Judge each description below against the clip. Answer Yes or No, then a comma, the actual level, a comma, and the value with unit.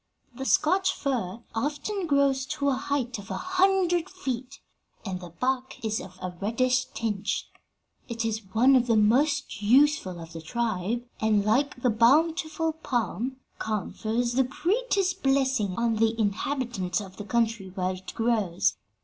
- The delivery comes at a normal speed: Yes, average, 150 wpm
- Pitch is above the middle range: Yes, high, 240 Hz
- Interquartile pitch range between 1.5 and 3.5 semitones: No, average, 5.0 semitones